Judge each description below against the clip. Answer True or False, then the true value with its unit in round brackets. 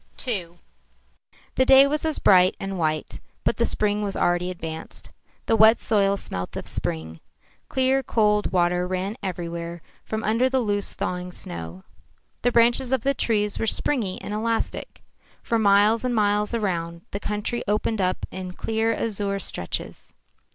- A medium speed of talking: True (155 wpm)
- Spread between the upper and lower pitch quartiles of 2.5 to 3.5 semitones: False (4.1 semitones)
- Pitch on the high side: True (205 Hz)